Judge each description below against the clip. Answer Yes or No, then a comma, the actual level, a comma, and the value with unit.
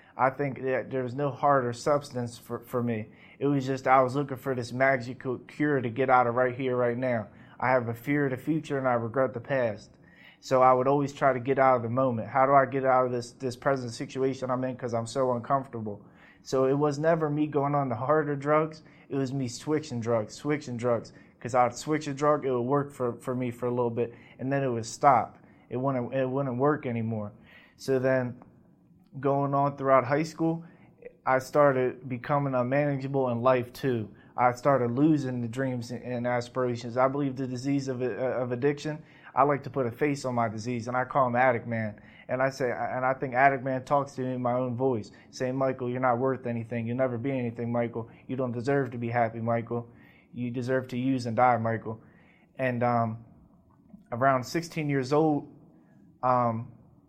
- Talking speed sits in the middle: No, fast, 210 wpm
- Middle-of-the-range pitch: No, low, 130 Hz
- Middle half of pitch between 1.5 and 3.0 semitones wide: Yes, narrow, 2.5 semitones